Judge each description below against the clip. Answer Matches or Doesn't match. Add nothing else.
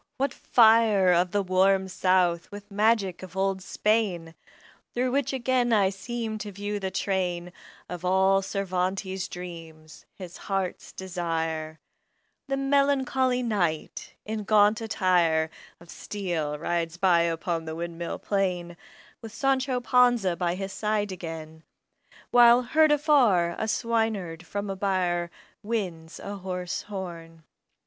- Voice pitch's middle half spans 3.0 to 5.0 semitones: Matches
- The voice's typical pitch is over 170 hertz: Matches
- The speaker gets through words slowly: Matches